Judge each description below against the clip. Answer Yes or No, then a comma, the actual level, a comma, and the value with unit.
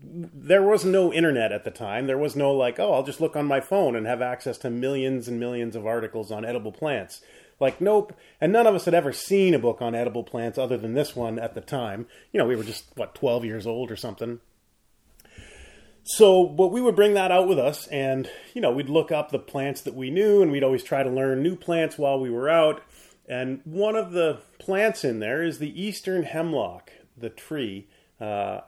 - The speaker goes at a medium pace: No, fast, 225 wpm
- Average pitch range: No, wide, 6.6 semitones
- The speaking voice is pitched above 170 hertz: No, medium, 140 Hz